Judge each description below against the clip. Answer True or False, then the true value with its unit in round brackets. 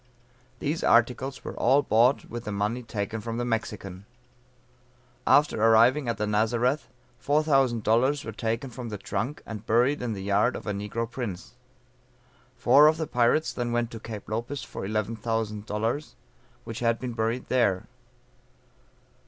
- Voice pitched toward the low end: True (115 Hz)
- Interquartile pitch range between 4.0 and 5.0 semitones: False (2.8 semitones)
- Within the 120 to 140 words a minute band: False (150 wpm)